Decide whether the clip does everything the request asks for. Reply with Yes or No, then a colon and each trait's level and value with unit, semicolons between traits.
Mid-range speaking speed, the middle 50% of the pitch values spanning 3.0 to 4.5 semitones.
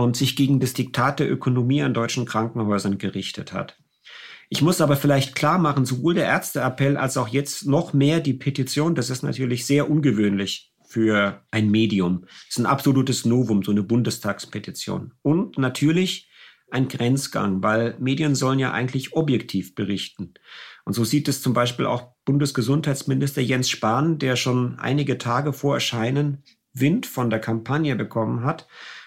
Yes: average, 160 wpm; average, 3.7 semitones